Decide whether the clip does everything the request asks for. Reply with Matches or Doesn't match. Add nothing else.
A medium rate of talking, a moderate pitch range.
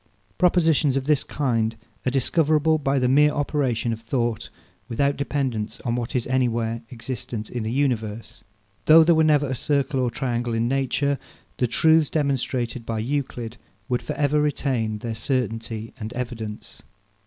Matches